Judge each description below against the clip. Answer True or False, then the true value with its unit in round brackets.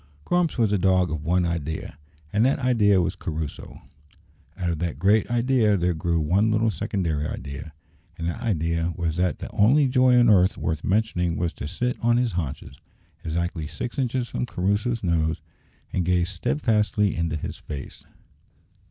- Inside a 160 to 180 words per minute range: True (170 wpm)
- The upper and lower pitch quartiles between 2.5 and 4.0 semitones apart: False (5.2 semitones)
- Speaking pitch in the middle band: False (90 Hz)